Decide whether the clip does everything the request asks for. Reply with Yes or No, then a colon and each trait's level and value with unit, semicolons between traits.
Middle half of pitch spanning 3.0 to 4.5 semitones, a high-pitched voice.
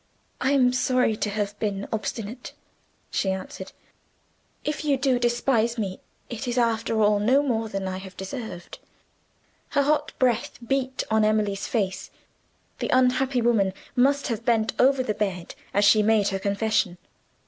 Yes: average, 3.8 semitones; high, 225 Hz